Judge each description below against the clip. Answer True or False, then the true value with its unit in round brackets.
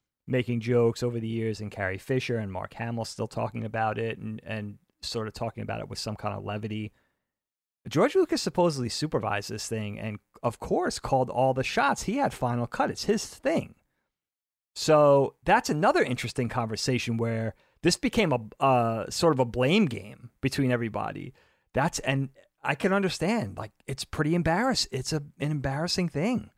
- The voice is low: True (120 Hz)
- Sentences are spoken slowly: False (175 wpm)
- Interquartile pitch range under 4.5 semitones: False (4.8 semitones)